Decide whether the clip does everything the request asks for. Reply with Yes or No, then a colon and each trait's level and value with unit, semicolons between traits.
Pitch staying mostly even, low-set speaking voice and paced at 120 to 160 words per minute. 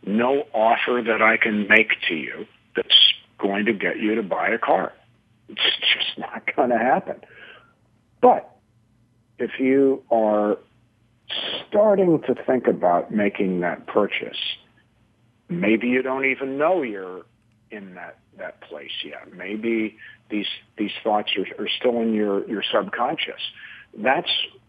No: average, 3.3 semitones; low, 115 Hz; average, 140 wpm